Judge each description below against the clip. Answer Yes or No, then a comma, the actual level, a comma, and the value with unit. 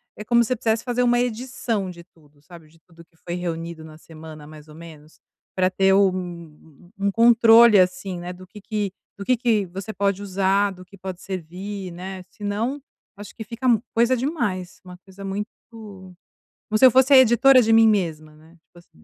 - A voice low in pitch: No, high, 195 Hz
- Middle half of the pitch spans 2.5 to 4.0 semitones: No, average, 4.6 semitones